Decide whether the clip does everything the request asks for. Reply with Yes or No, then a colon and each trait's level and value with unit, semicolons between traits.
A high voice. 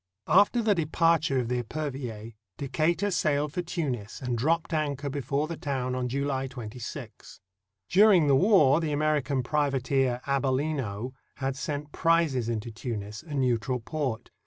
No: medium, 140 Hz